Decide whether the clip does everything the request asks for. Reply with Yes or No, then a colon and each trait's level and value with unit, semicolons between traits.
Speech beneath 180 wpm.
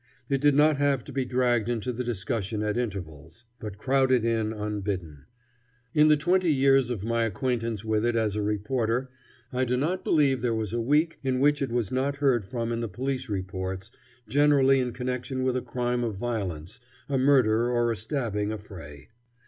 No: average, 190 wpm